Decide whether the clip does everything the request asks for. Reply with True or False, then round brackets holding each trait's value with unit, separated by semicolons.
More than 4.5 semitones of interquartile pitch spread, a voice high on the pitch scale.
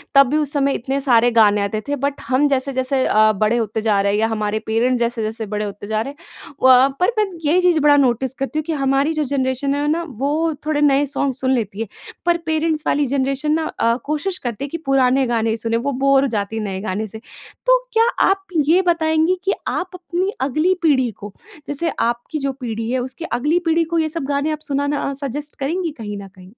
True (5.0 semitones; 275 Hz)